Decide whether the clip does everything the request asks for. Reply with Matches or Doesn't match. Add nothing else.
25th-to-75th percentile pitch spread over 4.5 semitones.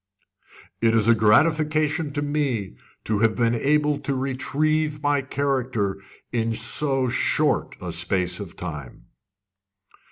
Matches